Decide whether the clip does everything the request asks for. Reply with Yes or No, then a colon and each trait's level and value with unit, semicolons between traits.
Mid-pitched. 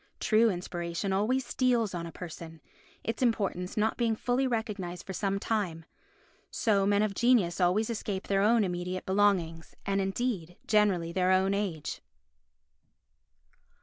No: high, 195 Hz